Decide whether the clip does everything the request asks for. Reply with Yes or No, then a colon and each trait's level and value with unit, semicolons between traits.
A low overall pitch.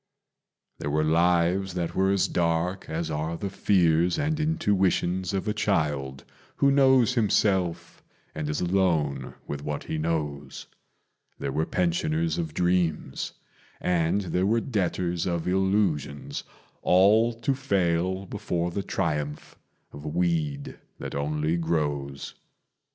Yes: very low, 85 Hz